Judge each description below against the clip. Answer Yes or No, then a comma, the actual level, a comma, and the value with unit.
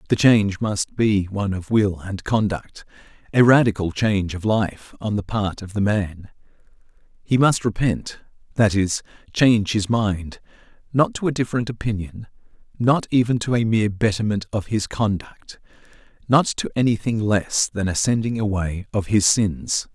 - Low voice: Yes, low, 105 Hz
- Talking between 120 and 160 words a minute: Yes, average, 145 wpm